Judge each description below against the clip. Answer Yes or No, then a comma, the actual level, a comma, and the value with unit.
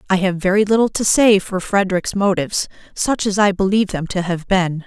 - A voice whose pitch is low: No, high, 195 Hz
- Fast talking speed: Yes, fast, 210 wpm